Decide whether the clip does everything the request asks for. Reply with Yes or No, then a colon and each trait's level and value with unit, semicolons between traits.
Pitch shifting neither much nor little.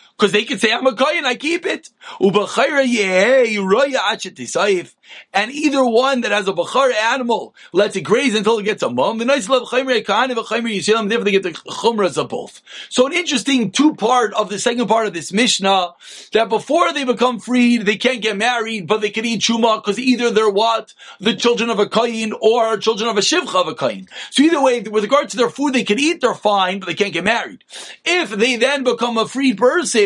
Yes: average, 3.5 semitones